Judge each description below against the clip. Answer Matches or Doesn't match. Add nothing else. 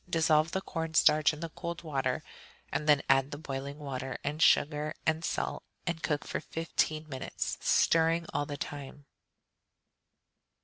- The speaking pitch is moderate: Matches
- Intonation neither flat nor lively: Doesn't match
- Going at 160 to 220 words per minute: Doesn't match